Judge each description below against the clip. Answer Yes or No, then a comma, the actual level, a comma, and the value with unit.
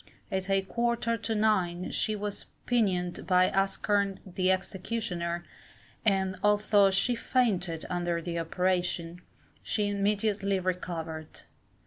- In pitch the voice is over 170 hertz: Yes, high, 190 Hz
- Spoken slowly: Yes, slow, 110 wpm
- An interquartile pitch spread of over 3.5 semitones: No, average, 2.7 semitones